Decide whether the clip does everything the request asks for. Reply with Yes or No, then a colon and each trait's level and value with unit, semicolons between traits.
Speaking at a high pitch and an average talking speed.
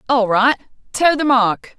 Yes: high, 245 Hz; average, 170 wpm